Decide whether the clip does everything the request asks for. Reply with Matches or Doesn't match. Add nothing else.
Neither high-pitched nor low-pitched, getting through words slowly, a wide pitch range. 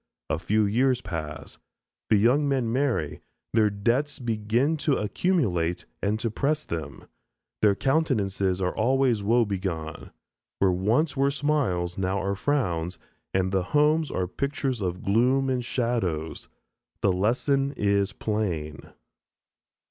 Doesn't match